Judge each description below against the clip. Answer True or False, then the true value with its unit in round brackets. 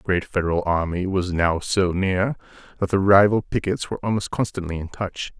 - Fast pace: False (190 wpm)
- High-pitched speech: False (95 Hz)